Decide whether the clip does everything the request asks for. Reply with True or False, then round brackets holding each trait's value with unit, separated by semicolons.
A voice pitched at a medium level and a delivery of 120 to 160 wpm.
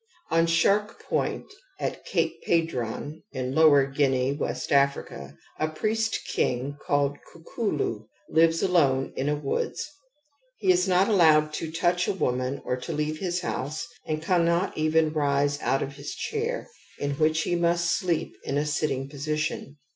True (155 Hz; 150 wpm)